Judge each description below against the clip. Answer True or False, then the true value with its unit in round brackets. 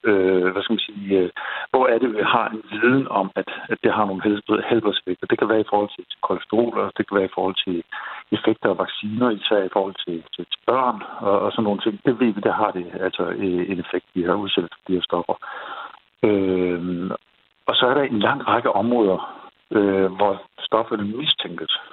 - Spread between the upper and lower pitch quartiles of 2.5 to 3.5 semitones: True (2.9 semitones)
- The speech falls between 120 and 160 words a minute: False (195 wpm)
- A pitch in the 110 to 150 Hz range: False (100 Hz)